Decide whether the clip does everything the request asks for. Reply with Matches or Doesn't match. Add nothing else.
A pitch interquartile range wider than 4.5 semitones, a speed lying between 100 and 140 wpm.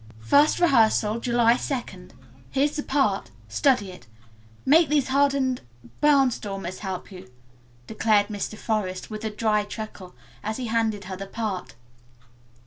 Matches